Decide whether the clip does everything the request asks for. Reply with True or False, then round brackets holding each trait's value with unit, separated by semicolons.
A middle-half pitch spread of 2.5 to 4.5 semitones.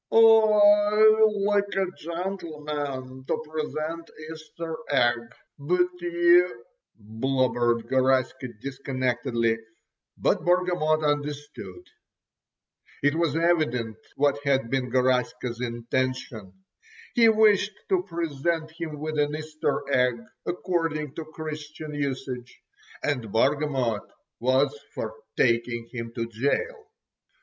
False (4.9 semitones)